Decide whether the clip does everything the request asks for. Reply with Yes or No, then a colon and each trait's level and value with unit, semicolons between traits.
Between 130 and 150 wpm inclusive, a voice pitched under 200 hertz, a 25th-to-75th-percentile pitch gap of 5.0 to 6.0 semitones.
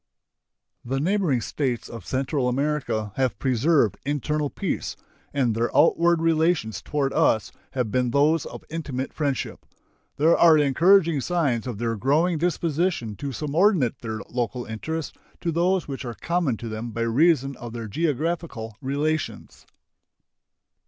Yes: average, 140 wpm; medium, 140 Hz; average, 5.3 semitones